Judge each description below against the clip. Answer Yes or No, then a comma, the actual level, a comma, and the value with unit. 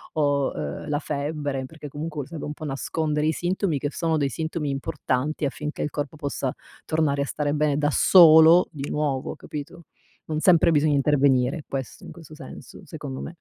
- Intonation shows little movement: Yes, narrow, 1.9 semitones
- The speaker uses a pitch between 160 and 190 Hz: No, medium, 150 Hz